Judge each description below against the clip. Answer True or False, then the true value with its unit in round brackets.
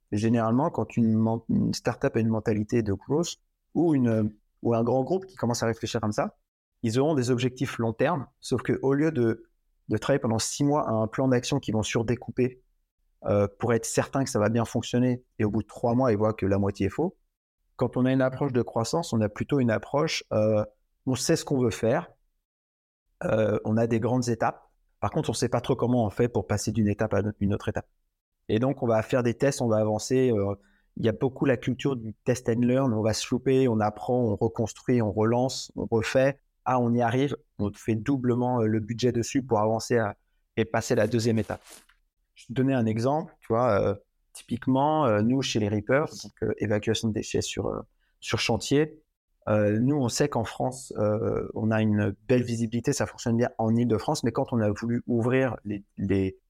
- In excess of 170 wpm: True (220 wpm)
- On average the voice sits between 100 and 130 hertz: True (115 Hz)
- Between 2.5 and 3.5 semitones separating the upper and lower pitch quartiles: True (3.0 semitones)